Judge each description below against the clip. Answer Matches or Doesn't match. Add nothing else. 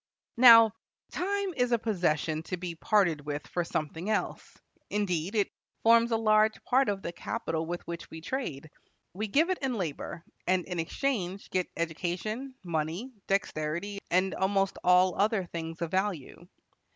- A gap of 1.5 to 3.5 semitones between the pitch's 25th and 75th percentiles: Doesn't match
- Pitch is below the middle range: Doesn't match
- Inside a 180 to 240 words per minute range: Doesn't match